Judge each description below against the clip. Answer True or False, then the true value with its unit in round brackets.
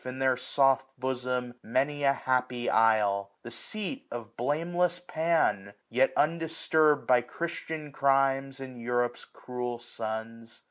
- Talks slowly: True (125 wpm)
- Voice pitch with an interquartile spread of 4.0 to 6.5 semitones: False (3.4 semitones)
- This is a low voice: True (130 Hz)